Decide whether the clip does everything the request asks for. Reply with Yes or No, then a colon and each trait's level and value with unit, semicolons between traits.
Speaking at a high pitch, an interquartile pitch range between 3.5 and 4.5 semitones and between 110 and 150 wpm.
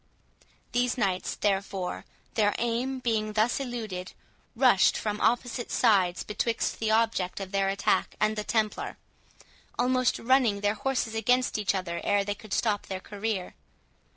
No: high, 215 Hz; average, 3.1 semitones; average, 145 wpm